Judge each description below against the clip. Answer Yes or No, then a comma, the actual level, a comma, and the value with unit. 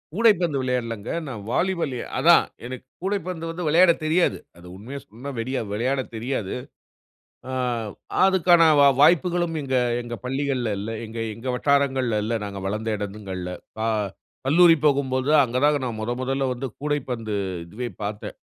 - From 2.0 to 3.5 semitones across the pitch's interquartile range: No, average, 4.8 semitones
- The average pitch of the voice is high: No, low, 130 Hz